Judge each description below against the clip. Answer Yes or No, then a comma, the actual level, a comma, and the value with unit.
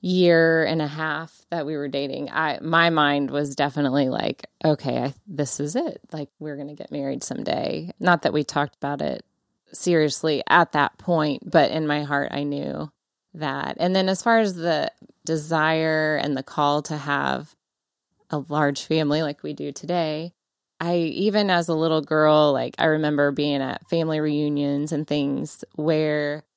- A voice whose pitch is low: No, medium, 155 Hz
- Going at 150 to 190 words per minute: Yes, average, 175 wpm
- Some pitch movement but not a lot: No, narrow, 2.3 semitones